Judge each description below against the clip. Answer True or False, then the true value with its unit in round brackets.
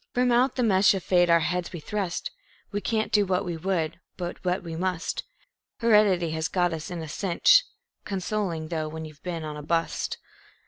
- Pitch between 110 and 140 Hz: False (180 Hz)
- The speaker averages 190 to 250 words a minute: True (195 wpm)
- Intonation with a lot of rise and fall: False (3.5 semitones)